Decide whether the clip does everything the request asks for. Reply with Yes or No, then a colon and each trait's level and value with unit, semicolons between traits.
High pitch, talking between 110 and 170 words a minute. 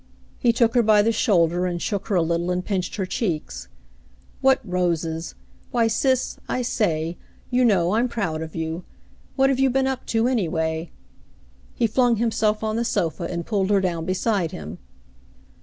No: high, 200 Hz; average, 185 wpm